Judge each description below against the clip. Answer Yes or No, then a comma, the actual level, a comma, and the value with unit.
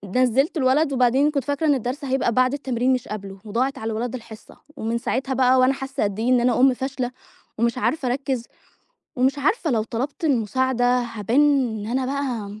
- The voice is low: No, very high, 255 Hz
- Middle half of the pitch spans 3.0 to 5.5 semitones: No, narrow, 2.6 semitones